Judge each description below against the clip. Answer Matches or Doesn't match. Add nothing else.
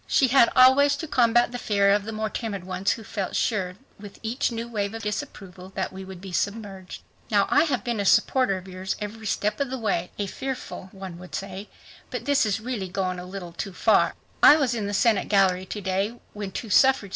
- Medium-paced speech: Doesn't match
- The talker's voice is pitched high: Matches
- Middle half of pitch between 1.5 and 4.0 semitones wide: Matches